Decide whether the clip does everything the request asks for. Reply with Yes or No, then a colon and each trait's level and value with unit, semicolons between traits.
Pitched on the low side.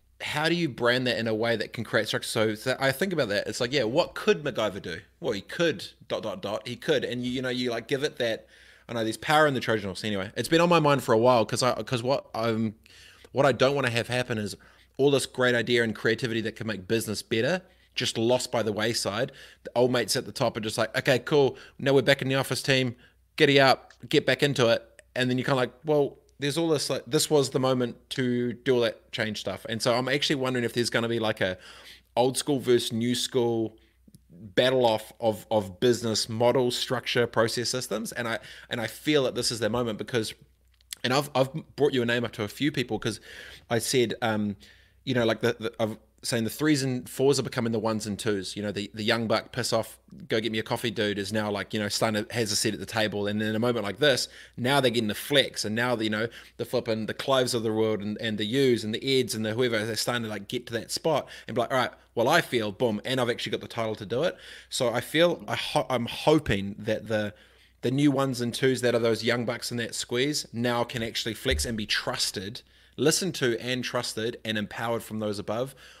Yes: low, 120 Hz